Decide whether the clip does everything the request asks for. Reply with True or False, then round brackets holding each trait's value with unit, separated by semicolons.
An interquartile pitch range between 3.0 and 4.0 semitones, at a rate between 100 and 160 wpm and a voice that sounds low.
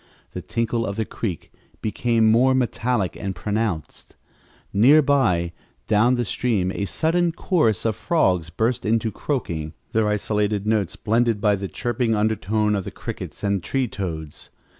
True (3.4 semitones; 150 wpm; 110 Hz)